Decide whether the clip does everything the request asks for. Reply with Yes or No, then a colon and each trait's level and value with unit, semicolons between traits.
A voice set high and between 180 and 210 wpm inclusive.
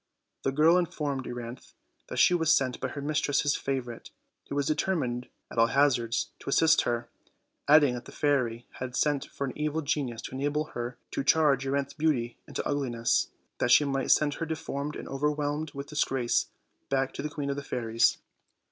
No: medium, 140 Hz; average, 185 wpm